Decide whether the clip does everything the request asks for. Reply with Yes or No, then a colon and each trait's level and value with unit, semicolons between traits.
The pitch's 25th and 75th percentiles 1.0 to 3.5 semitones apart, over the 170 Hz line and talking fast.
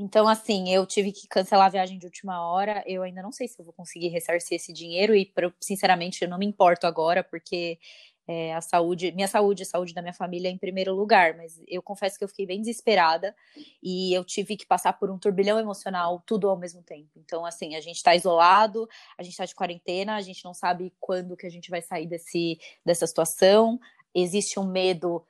Yes: narrow, 2.4 semitones; medium, 185 Hz; fast, 220 wpm